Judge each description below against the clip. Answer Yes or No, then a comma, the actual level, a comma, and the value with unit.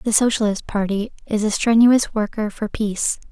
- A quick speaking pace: No, average, 165 wpm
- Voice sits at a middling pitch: No, high, 215 Hz